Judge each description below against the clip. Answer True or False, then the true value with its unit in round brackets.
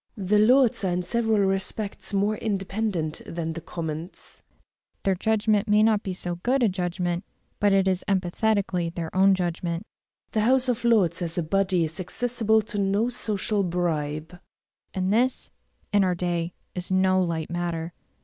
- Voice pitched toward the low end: False (190 Hz)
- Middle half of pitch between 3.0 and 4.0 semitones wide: True (3.6 semitones)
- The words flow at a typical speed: True (160 wpm)